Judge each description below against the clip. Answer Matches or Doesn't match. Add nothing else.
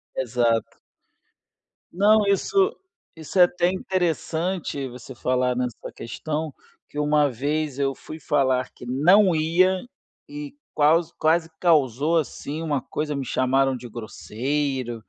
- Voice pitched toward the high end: Doesn't match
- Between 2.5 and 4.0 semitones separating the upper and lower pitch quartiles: Doesn't match